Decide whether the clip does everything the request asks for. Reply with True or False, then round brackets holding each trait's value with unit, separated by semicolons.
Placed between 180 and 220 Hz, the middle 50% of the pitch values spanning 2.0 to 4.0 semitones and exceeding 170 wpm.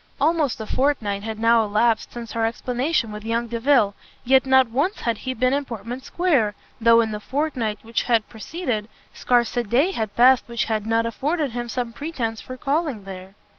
False (235 Hz; 3.1 semitones; 190 wpm)